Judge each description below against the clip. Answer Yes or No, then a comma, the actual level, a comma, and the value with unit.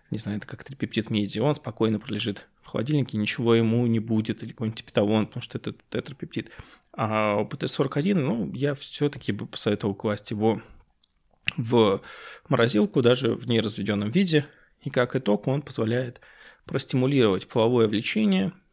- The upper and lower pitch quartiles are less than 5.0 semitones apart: Yes, average, 3.8 semitones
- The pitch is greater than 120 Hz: No, low, 115 Hz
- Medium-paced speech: Yes, average, 145 wpm